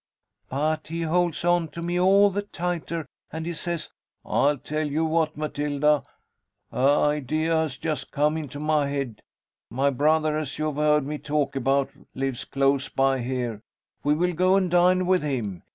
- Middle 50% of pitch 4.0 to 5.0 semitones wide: No, average, 3.1 semitones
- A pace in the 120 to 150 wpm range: No, average, 170 wpm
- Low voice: No, medium, 150 Hz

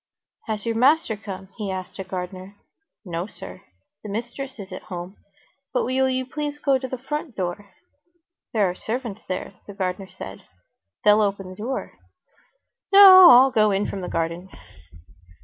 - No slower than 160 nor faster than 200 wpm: Yes, average, 165 wpm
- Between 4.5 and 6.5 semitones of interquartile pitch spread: Yes, wide, 5.6 semitones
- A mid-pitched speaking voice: No, high, 205 Hz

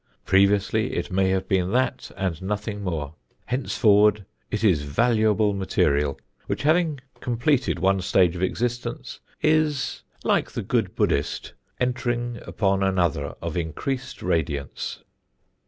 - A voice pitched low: Yes, low, 100 Hz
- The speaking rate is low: Yes, slow, 120 wpm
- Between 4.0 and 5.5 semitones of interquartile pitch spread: Yes, average, 5.0 semitones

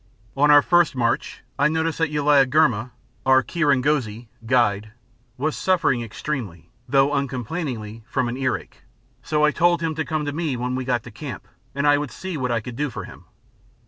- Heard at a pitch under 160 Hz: Yes, low, 135 Hz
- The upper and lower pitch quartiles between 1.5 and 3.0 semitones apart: No, average, 3.9 semitones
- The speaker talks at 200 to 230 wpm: No, average, 175 wpm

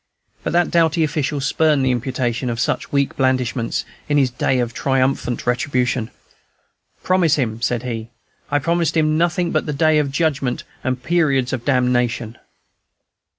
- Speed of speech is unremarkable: Yes, average, 150 wpm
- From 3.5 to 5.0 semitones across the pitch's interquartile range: Yes, average, 3.9 semitones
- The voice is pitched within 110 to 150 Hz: Yes, low, 135 Hz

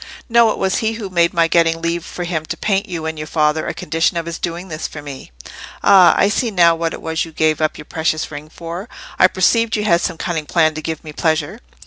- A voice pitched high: No, medium, 165 Hz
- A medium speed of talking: No, fast, 255 wpm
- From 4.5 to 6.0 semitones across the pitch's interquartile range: No, average, 2.9 semitones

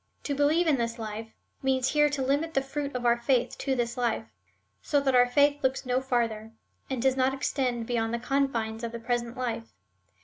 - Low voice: No, very high, 255 Hz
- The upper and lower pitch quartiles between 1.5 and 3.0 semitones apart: Yes, average, 2.7 semitones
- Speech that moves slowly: No, fast, 205 wpm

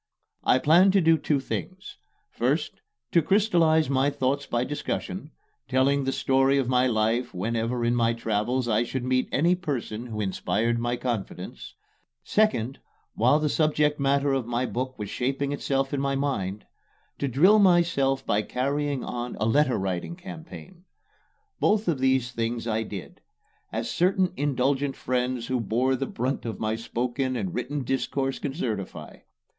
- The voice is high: No, low, 130 Hz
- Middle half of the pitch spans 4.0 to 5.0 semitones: No, average, 3.5 semitones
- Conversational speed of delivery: Yes, average, 155 wpm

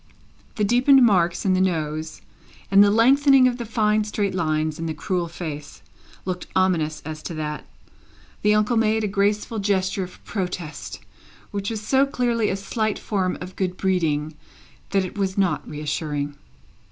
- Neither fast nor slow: Yes, average, 165 wpm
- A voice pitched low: No, high, 190 Hz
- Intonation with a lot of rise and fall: No, average, 4.5 semitones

